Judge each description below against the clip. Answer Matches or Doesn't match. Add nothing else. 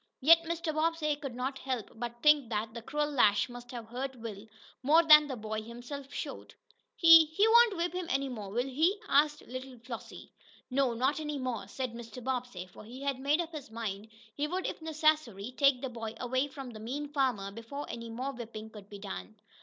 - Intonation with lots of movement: Doesn't match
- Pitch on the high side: Matches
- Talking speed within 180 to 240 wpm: Matches